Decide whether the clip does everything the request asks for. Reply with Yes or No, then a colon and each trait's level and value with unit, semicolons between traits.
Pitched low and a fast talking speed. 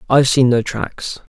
No: low, 125 Hz; average, 180 wpm